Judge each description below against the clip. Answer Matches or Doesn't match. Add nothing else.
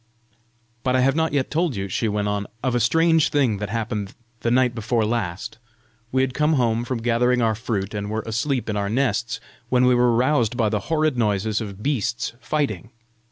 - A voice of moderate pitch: Doesn't match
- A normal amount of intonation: Matches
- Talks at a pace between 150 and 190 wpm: Doesn't match